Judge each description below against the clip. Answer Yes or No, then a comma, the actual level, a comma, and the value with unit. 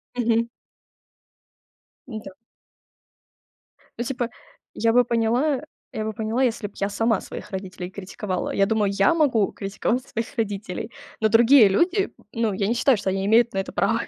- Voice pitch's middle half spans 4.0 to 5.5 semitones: No, average, 3.2 semitones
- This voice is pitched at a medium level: No, high, 225 Hz